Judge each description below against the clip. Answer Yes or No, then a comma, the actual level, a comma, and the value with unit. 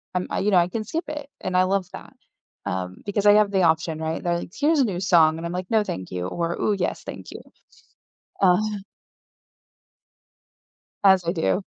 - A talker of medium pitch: Yes, medium, 180 Hz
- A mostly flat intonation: No, average, 3.6 semitones